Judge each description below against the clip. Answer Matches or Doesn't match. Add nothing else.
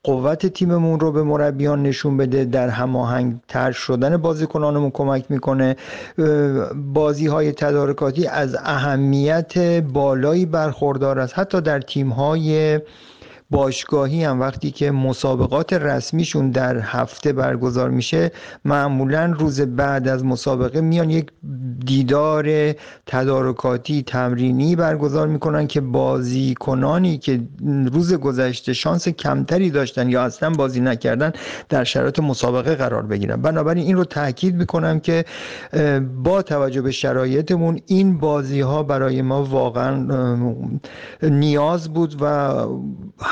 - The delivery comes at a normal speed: Matches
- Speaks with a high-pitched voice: Doesn't match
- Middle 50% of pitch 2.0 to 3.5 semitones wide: Matches